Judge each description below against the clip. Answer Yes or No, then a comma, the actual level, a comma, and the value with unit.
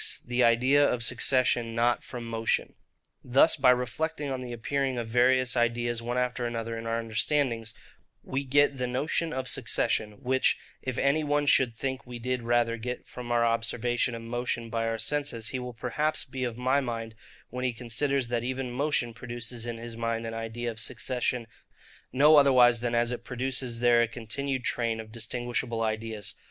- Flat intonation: Yes, narrow, 2.0 semitones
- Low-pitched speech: Yes, low, 120 Hz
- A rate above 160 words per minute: Yes, average, 180 wpm